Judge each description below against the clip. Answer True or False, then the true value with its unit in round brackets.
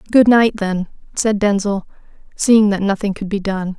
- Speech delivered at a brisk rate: False (175 wpm)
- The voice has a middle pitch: False (200 Hz)